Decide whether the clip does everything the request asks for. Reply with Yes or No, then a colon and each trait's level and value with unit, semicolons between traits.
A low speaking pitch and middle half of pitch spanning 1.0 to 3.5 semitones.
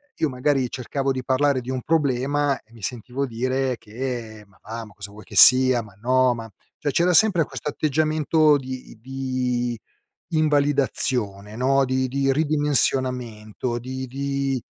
Yes: low, 130 Hz; narrow, 2.6 semitones